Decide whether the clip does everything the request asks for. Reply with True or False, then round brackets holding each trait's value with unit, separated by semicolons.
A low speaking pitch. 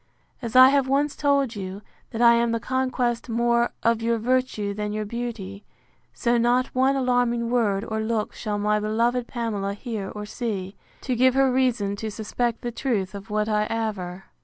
False (230 Hz)